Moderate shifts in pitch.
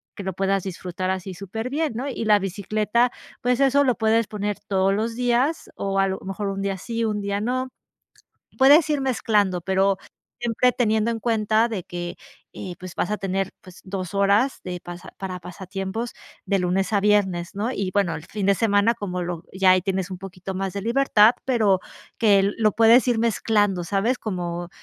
Yes: average, 3.2 semitones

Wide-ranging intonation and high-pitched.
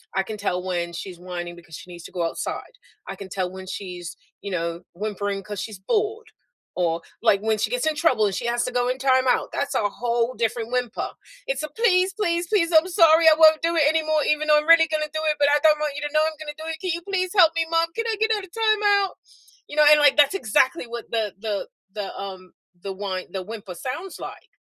Yes: wide, 8.6 semitones; very high, 265 Hz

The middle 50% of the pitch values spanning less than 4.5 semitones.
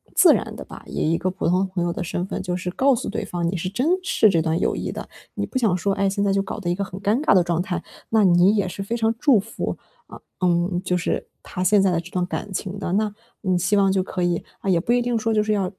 Yes: average, 2.8 semitones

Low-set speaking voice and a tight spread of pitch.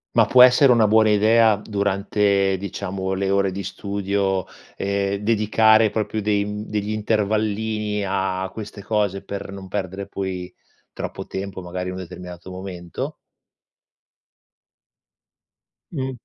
Yes: low, 100 Hz; narrow, 1.9 semitones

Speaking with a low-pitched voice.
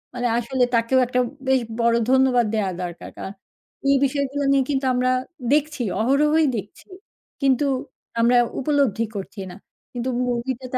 No: very high, 255 Hz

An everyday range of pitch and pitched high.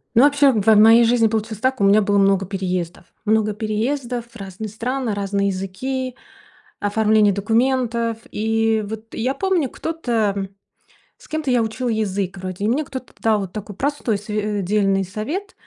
Yes: average, 3.5 semitones; high, 220 Hz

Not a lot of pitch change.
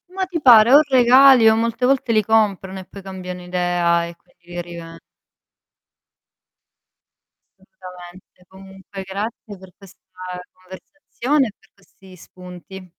No: average, 3.9 semitones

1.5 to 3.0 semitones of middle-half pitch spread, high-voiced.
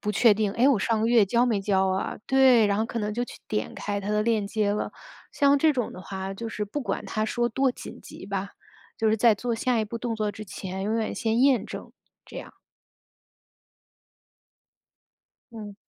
Yes: average, 2.7 semitones; high, 220 Hz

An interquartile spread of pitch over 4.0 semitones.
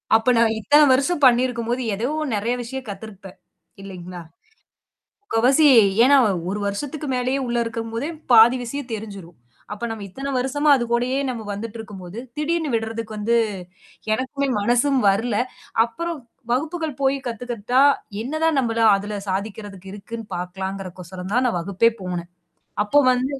Yes: average, 4.5 semitones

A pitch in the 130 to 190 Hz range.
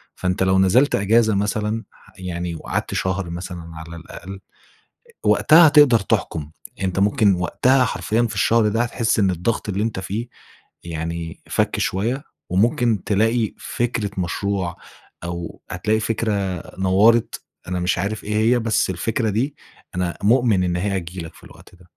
No: low, 100 Hz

